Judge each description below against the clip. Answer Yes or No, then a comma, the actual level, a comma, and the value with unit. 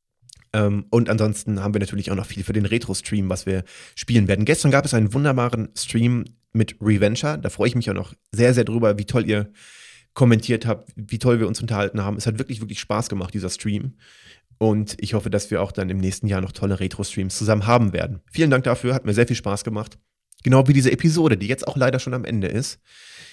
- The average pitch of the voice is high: No, low, 110 Hz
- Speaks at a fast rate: Yes, fast, 225 wpm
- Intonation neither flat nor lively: Yes, average, 3.0 semitones